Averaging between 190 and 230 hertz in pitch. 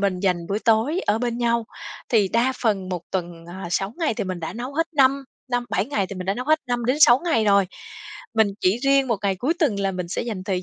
Yes: high, 220 Hz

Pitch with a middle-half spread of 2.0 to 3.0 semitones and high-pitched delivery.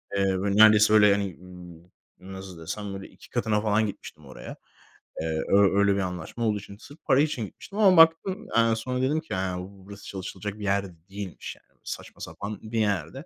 No: average, 2.7 semitones; low, 100 Hz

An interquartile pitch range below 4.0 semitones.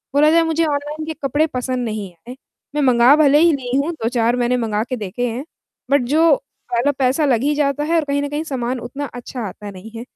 Yes: average, 3.6 semitones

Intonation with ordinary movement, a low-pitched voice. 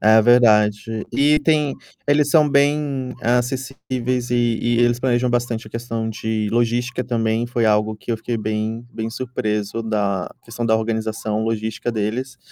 No: narrow, 2.1 semitones; low, 115 Hz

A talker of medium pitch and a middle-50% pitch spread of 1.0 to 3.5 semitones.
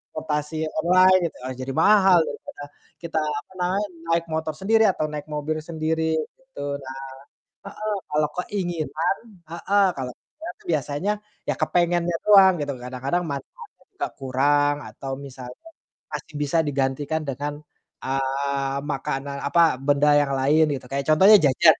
No: medium, 150 Hz; average, 4.3 semitones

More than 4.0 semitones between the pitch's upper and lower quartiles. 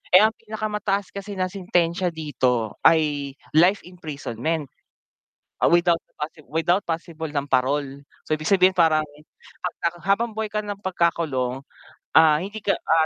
Yes: average, 4.5 semitones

